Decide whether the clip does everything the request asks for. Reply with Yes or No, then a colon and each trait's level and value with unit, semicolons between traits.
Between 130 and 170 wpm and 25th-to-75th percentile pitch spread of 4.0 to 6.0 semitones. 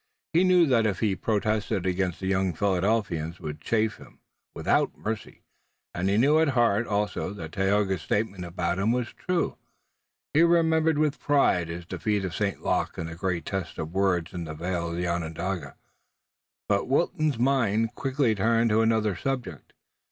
Yes: average, 165 wpm; average, 4.9 semitones